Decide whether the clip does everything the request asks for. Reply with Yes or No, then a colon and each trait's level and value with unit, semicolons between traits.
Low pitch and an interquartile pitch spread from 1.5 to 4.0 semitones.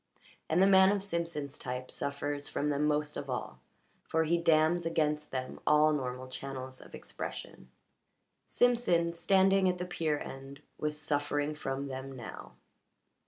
No: medium, 150 Hz; average, 3.7 semitones